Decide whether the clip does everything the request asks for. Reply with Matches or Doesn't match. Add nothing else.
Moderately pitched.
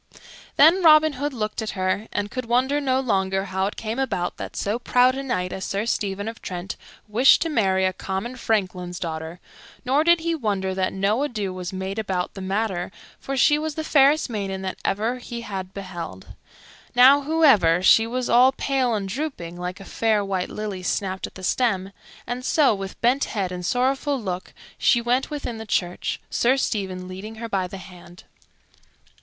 Doesn't match